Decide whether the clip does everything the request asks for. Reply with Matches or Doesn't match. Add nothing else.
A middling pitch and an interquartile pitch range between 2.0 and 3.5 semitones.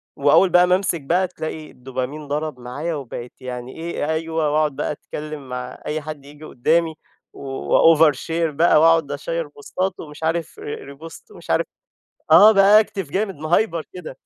Matches